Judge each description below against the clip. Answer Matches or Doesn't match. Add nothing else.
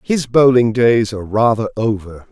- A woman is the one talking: Doesn't match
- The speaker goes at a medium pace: Matches